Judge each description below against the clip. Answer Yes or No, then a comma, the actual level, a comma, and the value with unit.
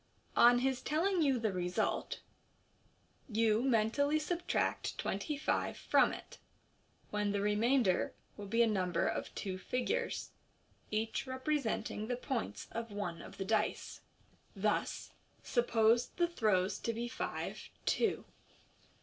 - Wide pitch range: No, average, 4.0 semitones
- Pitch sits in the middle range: No, high, 230 Hz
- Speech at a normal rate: No, slow, 125 wpm